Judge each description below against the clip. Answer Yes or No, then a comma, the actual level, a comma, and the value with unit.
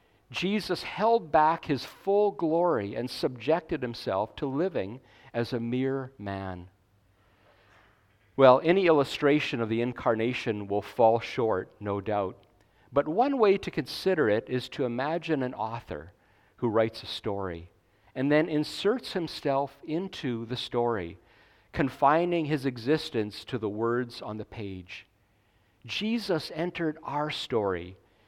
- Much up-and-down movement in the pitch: Yes, wide, 6.7 semitones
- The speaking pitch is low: Yes, low, 120 Hz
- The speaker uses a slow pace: Yes, slow, 130 wpm